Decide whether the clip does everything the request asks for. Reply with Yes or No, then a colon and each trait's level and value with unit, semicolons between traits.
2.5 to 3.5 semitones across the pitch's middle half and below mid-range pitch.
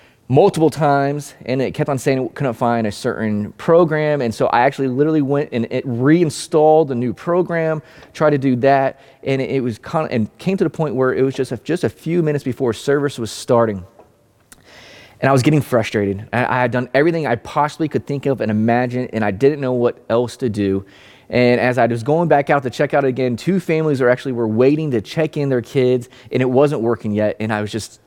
No: average, 3.9 semitones; low, 130 Hz